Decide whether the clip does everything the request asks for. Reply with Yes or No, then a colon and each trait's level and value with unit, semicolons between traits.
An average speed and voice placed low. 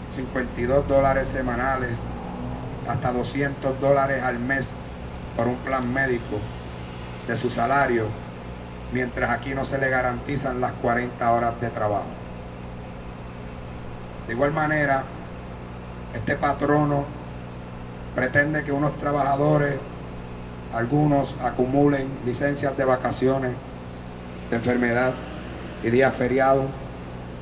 No: slow, 100 wpm; low, 120 Hz